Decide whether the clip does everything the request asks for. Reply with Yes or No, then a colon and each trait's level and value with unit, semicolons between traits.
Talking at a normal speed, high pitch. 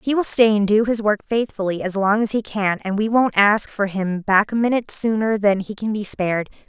No: fast, 250 wpm; high, 210 Hz